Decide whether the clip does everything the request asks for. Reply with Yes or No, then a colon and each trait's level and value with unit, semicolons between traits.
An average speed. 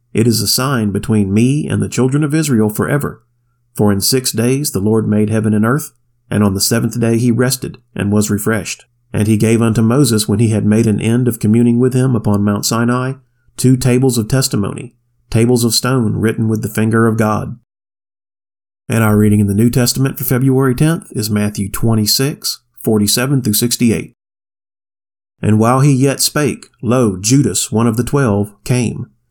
Yes: average, 180 wpm